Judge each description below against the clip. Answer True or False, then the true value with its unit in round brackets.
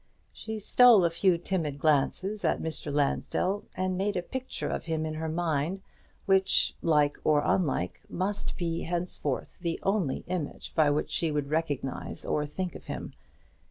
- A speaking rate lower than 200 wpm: True (160 wpm)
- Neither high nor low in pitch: True (165 Hz)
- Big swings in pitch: False (4.0 semitones)